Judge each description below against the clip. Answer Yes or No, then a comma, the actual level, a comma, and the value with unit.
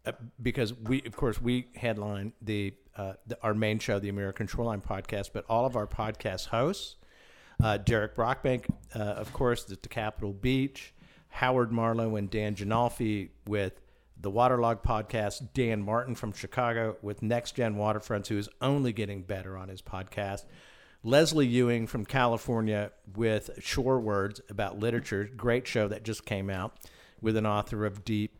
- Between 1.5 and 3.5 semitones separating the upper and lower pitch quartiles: Yes, narrow, 2.6 semitones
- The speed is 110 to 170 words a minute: Yes, average, 165 wpm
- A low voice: Yes, low, 110 Hz